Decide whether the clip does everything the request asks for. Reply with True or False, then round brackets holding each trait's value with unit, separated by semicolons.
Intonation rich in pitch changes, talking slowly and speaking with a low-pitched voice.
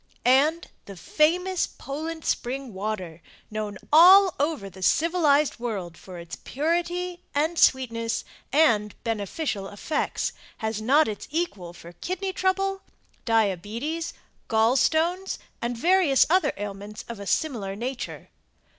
False (7.9 semitones; 120 wpm; 260 Hz)